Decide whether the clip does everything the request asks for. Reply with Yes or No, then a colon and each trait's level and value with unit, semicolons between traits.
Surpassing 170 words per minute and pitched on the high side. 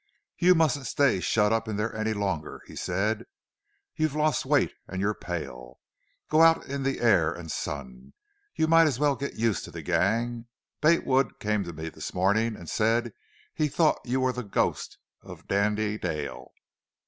No: average, 180 wpm; low, 110 Hz